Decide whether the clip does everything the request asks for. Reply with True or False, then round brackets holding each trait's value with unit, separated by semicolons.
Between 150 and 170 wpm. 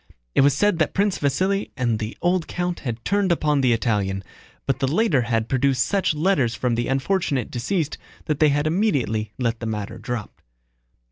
False (185 wpm)